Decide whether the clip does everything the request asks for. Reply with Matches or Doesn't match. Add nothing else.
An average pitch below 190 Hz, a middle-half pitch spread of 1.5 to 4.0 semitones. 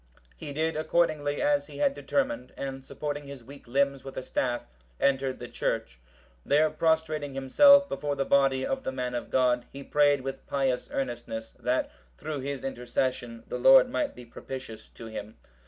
Matches